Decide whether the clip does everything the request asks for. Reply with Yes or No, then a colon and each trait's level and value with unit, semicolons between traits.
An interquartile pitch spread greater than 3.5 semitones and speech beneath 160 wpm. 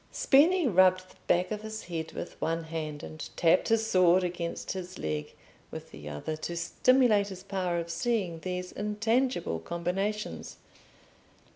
Yes: average, 4.1 semitones; average, 150 wpm